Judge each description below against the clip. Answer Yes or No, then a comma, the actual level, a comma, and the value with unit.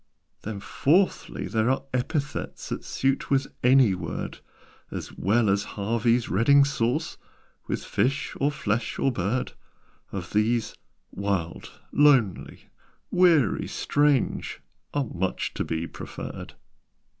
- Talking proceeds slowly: Yes, slow, 115 wpm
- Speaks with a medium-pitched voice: No, low, 120 Hz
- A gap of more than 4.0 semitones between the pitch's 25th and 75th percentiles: Yes, wide, 5.4 semitones